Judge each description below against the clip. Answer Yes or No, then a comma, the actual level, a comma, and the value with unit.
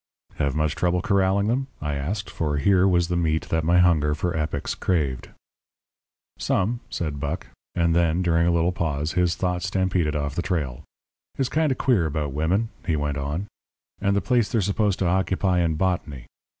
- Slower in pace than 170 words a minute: No, average, 185 wpm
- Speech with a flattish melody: No, average, 3.6 semitones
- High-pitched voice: No, very low, 85 Hz